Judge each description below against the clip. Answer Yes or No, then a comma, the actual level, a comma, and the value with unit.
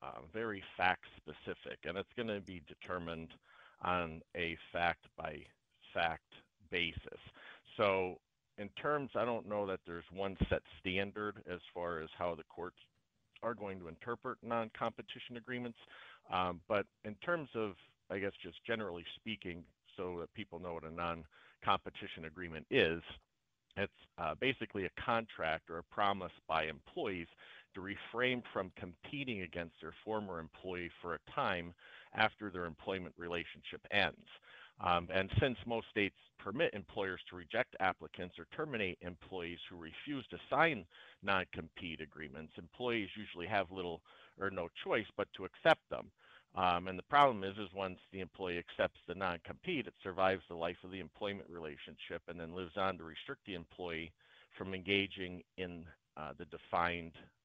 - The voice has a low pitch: Yes, very low, 90 Hz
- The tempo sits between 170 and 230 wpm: No, average, 155 wpm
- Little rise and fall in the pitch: No, average, 3.5 semitones